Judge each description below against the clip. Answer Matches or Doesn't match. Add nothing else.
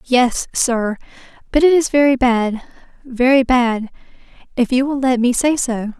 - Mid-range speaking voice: Doesn't match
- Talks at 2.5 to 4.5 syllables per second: Matches